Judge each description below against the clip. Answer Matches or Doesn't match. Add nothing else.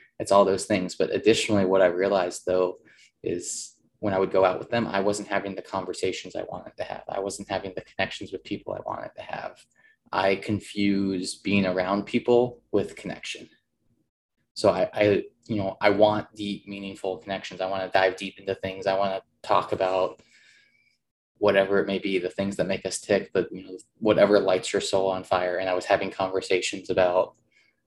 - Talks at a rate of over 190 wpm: Matches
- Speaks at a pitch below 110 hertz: Matches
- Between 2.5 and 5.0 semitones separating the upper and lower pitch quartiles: Doesn't match